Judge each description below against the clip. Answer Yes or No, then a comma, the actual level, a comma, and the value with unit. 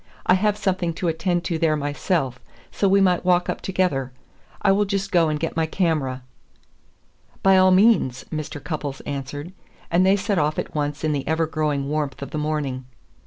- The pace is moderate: Yes, average, 190 wpm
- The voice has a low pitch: No, medium, 160 Hz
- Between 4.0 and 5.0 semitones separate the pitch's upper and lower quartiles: Yes, average, 4.4 semitones